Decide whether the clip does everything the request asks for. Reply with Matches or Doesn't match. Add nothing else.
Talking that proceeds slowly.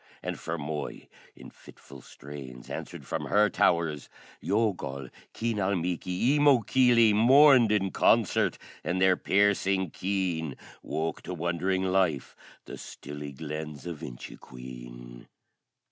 Matches